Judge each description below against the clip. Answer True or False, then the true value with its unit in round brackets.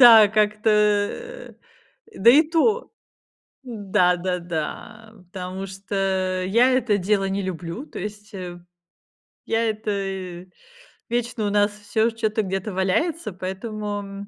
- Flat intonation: False (3.0 semitones)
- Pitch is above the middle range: True (210 Hz)